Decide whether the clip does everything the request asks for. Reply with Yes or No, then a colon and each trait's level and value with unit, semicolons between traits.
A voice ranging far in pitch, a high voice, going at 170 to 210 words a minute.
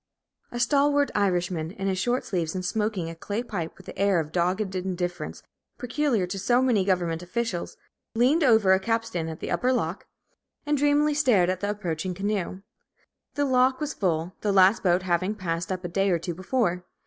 No: average, 5.0 semitones; high, 195 Hz; average, 190 wpm